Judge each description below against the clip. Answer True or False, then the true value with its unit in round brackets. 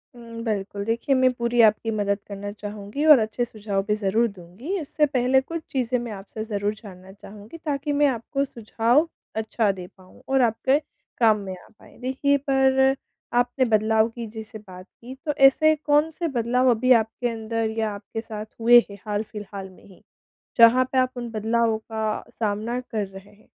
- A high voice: True (225 Hz)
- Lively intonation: False (3.6 semitones)